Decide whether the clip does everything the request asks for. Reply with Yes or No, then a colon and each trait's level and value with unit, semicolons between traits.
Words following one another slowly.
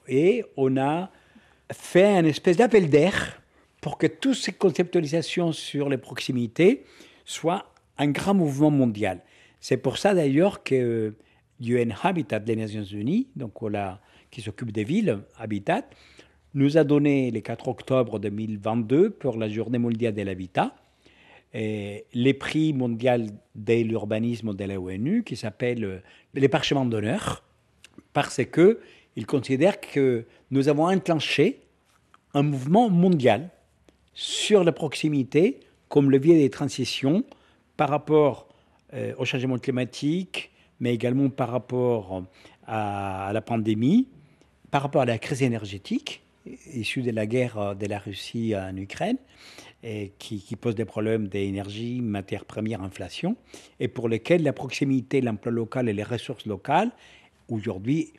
Yes: slow, 135 wpm